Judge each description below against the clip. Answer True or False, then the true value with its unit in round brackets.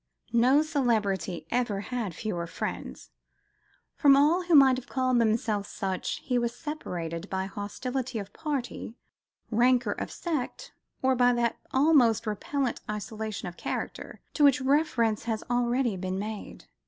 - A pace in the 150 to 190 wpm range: False (140 wpm)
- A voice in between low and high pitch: False (240 Hz)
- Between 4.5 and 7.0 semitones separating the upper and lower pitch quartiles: False (4.1 semitones)